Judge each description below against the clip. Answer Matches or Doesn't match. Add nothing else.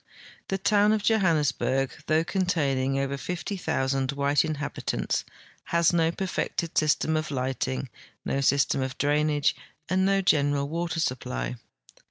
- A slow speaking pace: Matches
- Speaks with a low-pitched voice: Doesn't match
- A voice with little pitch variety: Doesn't match